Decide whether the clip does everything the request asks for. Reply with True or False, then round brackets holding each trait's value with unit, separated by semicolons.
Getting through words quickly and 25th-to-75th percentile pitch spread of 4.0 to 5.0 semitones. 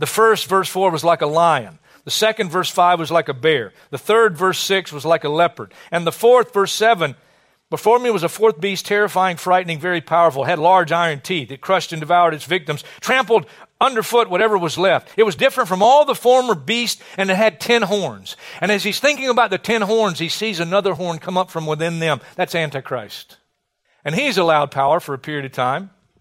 True (220 wpm; 4.7 semitones)